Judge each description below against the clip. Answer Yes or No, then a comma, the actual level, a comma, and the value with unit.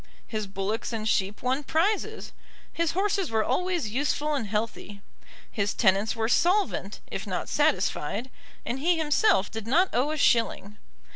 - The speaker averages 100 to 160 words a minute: Yes, average, 150 wpm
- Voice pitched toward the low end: No, very high, 250 Hz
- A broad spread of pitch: Yes, wide, 7.3 semitones